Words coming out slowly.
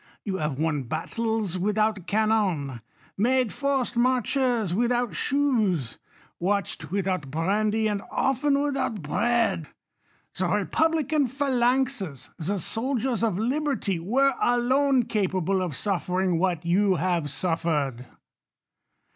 Yes: slow, 105 wpm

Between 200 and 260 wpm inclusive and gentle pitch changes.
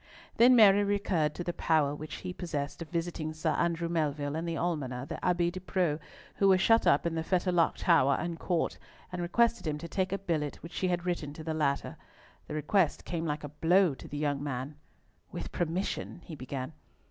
No: fast, 205 wpm; average, 3.2 semitones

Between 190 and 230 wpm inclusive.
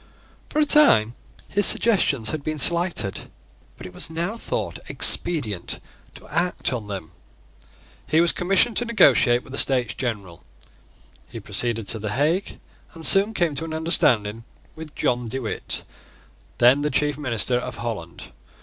No: average, 155 wpm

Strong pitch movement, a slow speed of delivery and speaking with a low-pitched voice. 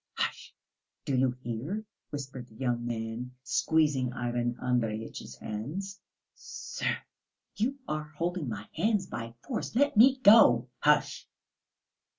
Yes: wide, 6.8 semitones; slow, 120 wpm; low, 130 Hz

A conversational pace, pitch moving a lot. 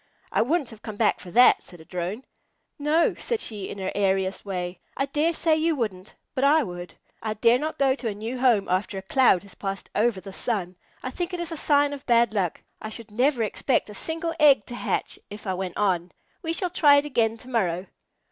No: fast, 230 wpm; wide, 6.7 semitones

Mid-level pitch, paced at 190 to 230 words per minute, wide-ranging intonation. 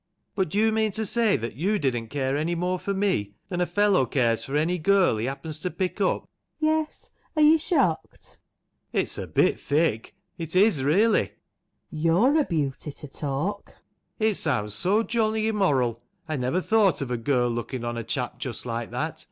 Yes: medium, 165 Hz; average, 200 wpm; wide, 8.0 semitones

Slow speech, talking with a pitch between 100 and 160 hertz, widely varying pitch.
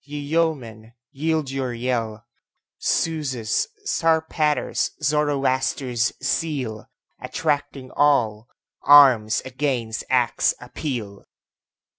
No: slow, 75 wpm; low, 135 Hz; average, 4.0 semitones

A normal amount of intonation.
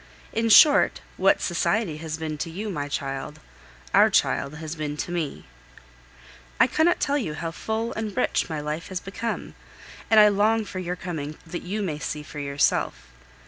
No: wide, 5.8 semitones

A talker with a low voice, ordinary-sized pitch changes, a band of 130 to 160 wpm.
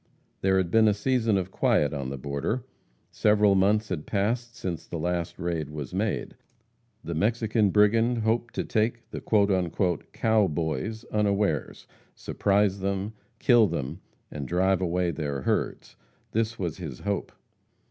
Yes: low, 100 Hz; average, 4.4 semitones; average, 145 wpm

